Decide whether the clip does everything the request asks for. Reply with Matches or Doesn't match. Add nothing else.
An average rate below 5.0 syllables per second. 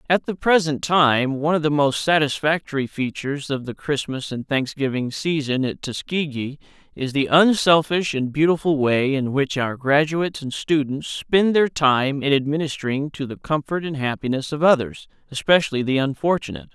Doesn't match